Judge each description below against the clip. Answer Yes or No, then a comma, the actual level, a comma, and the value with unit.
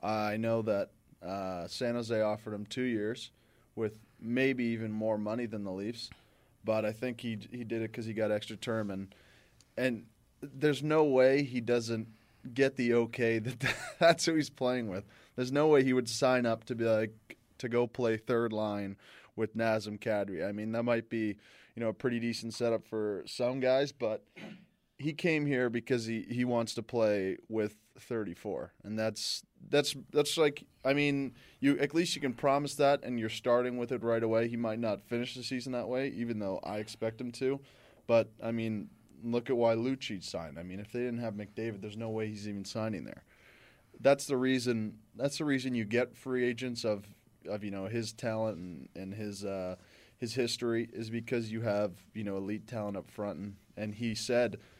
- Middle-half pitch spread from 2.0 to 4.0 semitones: Yes, average, 2.8 semitones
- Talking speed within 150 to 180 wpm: No, average, 200 wpm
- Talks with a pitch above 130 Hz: No, low, 115 Hz